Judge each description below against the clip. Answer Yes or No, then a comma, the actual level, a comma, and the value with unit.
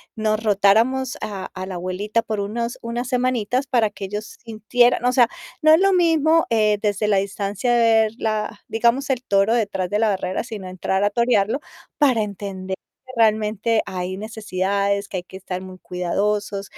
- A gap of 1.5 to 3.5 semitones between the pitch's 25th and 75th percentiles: Yes, average, 3.1 semitones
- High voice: Yes, high, 215 Hz